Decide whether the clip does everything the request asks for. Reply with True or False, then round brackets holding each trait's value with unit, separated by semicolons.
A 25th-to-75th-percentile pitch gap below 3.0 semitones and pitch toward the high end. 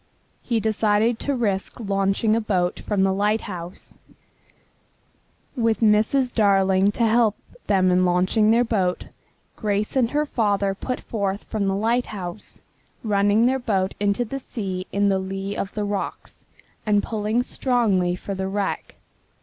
True (2.6 semitones; 205 Hz)